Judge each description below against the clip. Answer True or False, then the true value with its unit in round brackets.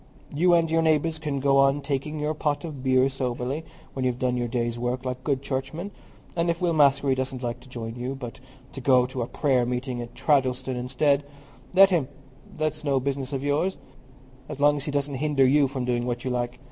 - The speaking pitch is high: False (135 Hz)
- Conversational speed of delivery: False (215 wpm)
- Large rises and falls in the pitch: False (2.8 semitones)